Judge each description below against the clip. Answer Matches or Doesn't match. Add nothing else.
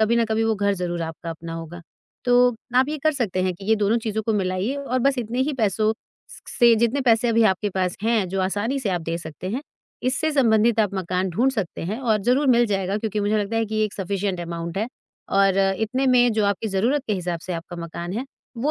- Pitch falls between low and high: Doesn't match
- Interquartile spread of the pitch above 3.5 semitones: Matches